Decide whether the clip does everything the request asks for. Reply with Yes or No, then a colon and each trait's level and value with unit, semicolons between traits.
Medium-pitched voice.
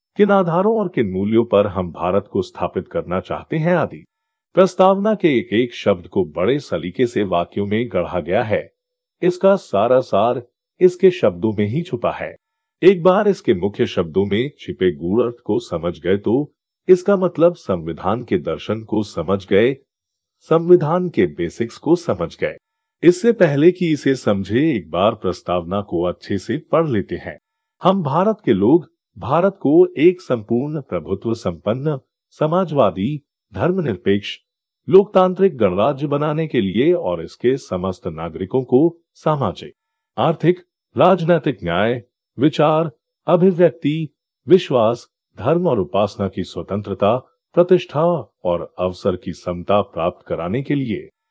Yes: medium, 155 Hz